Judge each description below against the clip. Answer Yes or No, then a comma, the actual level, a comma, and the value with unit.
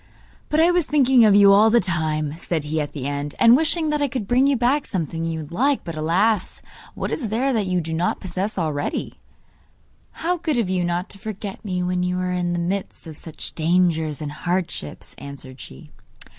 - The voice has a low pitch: No, medium, 180 Hz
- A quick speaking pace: Yes, fast, 210 wpm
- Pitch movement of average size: No, wide, 6.5 semitones